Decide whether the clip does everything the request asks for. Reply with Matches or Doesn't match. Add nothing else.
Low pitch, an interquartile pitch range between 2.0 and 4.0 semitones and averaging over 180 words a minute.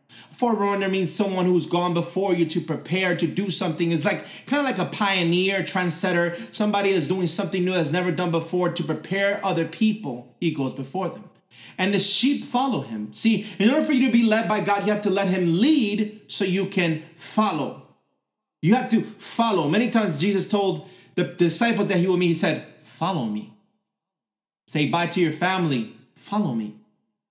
Doesn't match